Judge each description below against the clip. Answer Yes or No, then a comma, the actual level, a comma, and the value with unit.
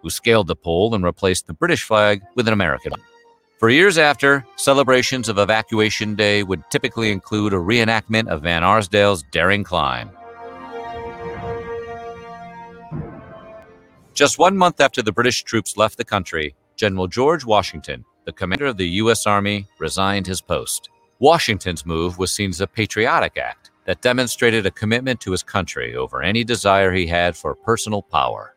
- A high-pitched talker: No, low, 110 Hz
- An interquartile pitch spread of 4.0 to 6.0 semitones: Yes, average, 5.1 semitones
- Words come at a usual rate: Yes, average, 160 wpm